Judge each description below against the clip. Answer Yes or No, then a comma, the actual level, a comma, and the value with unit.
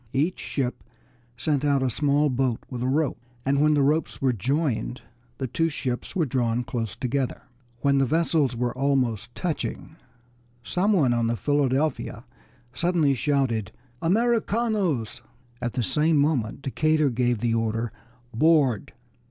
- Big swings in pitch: No, average, 4.1 semitones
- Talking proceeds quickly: No, average, 145 wpm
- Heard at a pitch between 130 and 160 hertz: Yes, low, 135 Hz